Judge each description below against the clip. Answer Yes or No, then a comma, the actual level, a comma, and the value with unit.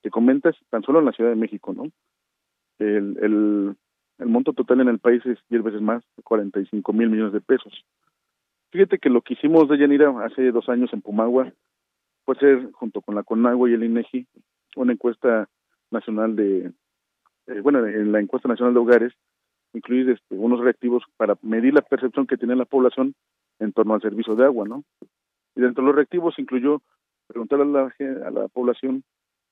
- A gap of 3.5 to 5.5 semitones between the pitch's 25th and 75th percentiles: No, average, 3.0 semitones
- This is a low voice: Yes, low, 120 Hz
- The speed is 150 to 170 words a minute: No, average, 185 wpm